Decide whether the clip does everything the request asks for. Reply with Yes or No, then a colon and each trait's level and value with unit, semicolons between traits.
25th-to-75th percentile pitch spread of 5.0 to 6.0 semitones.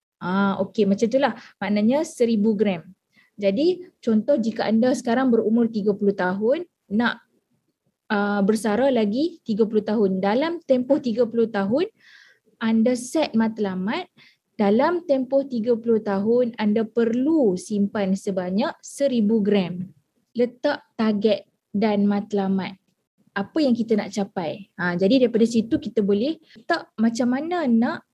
No: average, 3.7 semitones